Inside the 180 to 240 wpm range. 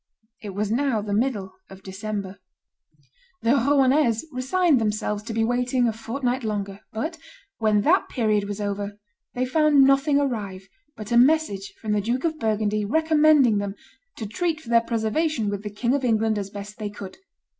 No: average, 170 wpm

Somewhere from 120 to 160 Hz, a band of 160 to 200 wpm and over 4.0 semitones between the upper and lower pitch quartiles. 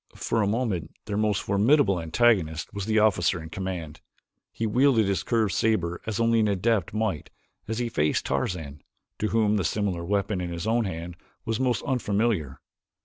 No: low, 100 Hz; average, 175 wpm; average, 4.4 semitones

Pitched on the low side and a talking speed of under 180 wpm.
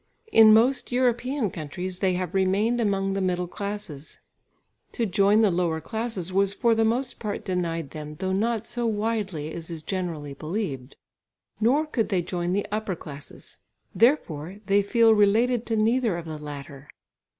No: high, 195 Hz; average, 160 wpm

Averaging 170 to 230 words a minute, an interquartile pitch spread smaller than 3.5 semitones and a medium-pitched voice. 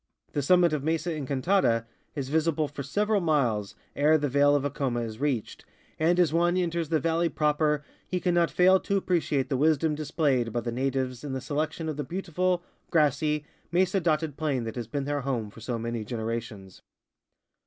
No: average, 185 wpm; average, 4.3 semitones; medium, 150 Hz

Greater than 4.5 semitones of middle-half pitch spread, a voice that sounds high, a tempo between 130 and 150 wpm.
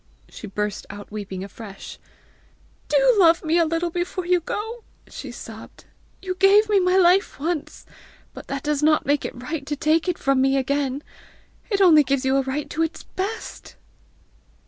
No: average, 5.2 semitones; very high, 310 Hz; average, 175 wpm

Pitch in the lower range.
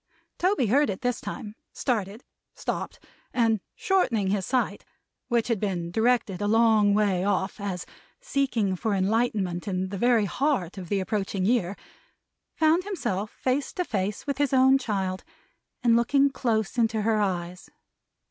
No: high, 220 Hz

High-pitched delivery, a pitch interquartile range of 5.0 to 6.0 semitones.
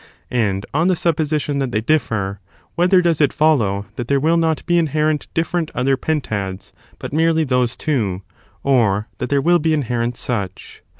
No: medium, 140 Hz; wide, 5.5 semitones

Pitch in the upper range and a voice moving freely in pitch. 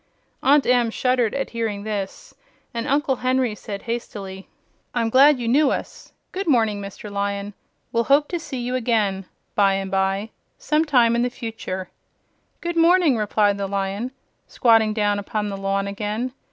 No: high, 225 Hz; average, 4.2 semitones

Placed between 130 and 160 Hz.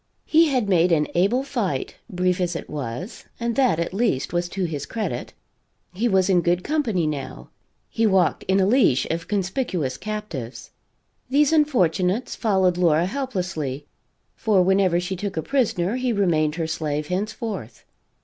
No: medium, 185 Hz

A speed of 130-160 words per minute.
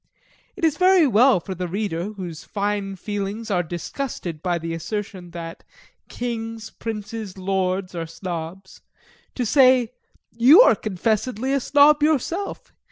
Yes: slow, 135 wpm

